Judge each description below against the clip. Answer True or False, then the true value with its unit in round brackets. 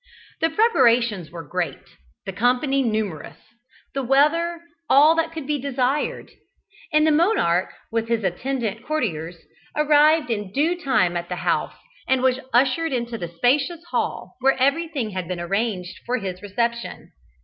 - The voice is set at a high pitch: True (250 Hz)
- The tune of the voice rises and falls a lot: True (7.3 semitones)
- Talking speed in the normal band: True (150 wpm)